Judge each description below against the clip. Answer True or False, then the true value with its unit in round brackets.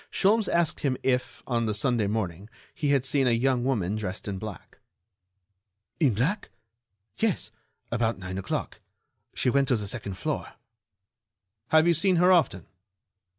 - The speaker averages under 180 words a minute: True (150 wpm)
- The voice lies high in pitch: False (125 Hz)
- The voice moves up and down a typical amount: False (6.1 semitones)